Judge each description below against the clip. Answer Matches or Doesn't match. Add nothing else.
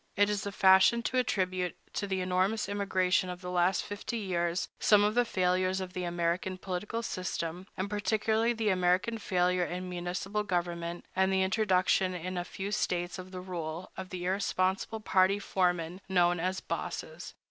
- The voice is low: Doesn't match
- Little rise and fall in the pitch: Matches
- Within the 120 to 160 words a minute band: Doesn't match